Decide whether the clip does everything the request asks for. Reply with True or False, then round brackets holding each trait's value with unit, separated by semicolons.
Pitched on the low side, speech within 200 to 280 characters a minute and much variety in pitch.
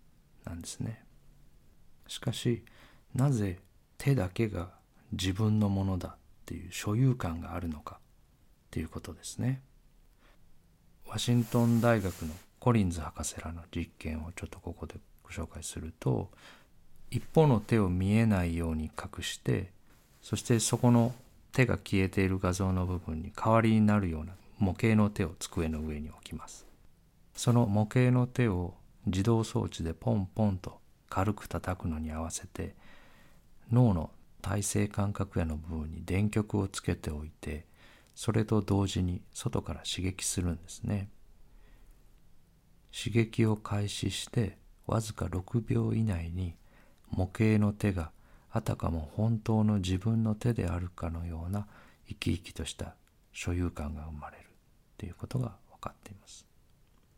False (100 Hz; 275 characters per minute; 4.7 semitones)